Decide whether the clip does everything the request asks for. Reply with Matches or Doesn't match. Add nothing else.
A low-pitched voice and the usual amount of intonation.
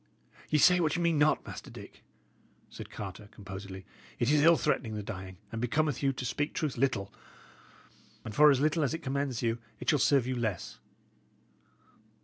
Doesn't match